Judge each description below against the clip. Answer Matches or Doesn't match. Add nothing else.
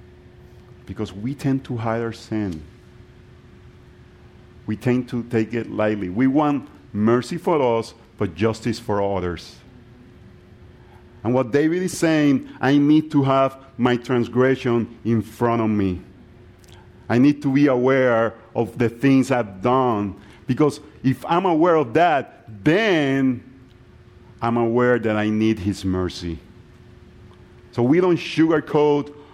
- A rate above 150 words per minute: Doesn't match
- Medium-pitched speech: Doesn't match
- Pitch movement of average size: Matches